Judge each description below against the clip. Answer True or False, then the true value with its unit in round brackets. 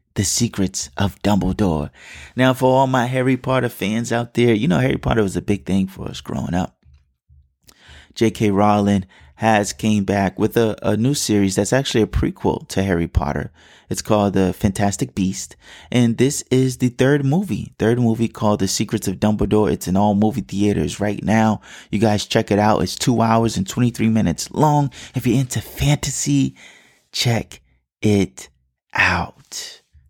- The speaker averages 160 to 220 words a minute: True (170 wpm)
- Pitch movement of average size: True (3.8 semitones)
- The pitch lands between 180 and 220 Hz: False (105 Hz)